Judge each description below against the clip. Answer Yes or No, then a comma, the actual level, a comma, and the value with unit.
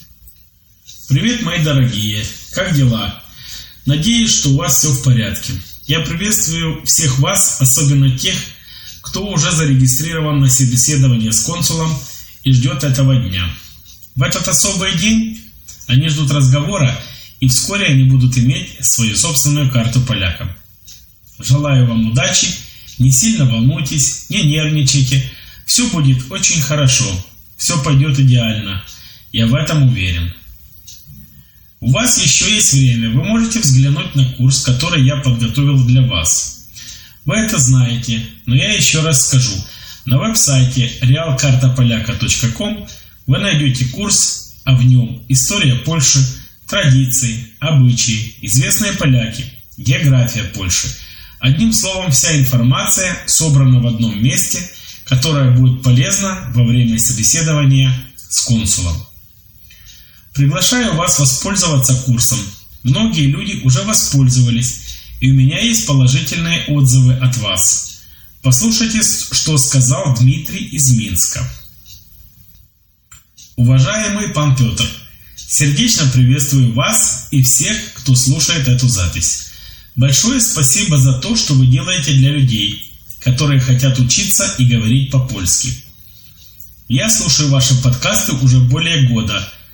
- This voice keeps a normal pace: Yes, average, 120 wpm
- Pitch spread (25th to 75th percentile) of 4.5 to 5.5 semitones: No, average, 3.9 semitones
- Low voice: Yes, low, 130 Hz